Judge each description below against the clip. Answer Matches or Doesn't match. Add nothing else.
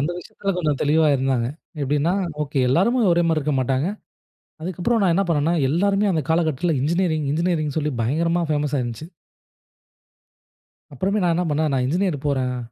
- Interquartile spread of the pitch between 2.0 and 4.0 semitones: Matches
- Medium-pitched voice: Matches